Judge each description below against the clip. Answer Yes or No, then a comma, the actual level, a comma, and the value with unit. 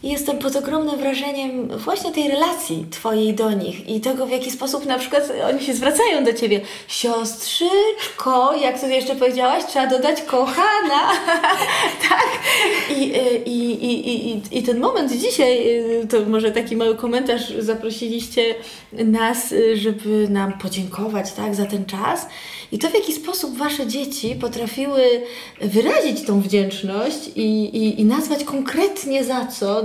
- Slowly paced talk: No, average, 145 wpm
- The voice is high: Yes, very high, 250 Hz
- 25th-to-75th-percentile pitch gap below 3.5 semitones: No, average, 4.0 semitones